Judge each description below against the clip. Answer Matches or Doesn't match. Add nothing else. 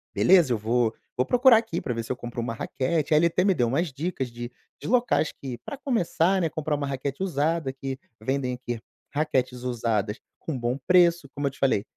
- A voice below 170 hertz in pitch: Matches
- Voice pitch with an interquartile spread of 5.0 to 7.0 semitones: Matches